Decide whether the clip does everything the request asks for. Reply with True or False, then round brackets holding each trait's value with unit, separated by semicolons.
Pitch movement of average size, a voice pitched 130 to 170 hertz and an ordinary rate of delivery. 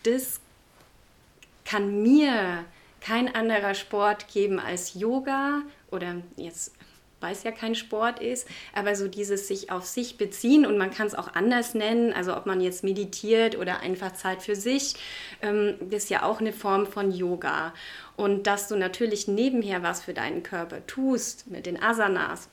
False (3.0 semitones; 210 Hz; 165 wpm)